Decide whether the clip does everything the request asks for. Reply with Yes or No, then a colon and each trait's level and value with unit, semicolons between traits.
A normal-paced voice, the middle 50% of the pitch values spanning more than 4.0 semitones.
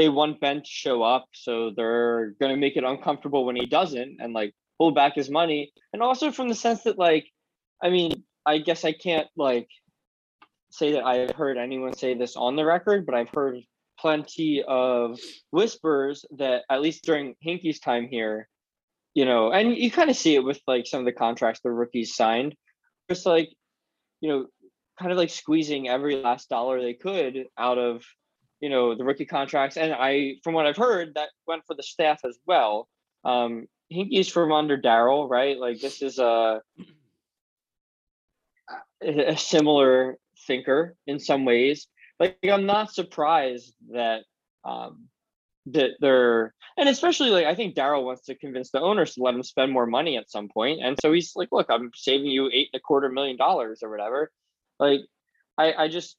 Yes: average, 185 wpm; average, 4.4 semitones